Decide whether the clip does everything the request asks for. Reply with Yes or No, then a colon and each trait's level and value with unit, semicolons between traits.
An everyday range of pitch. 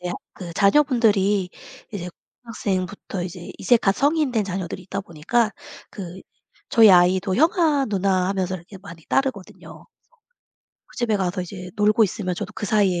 Yes: average, 3.4 semitones